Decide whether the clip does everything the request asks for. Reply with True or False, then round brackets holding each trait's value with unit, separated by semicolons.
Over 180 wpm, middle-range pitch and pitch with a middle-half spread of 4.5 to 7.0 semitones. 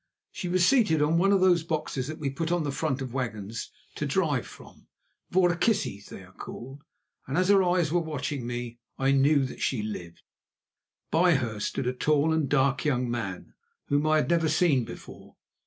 True (190 wpm; 145 Hz; 5.0 semitones)